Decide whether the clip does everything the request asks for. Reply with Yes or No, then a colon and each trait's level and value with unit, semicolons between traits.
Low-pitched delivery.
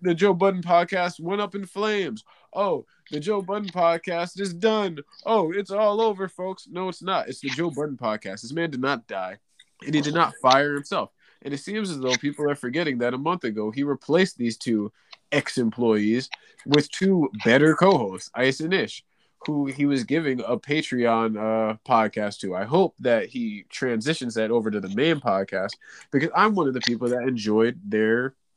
No: medium, 145 Hz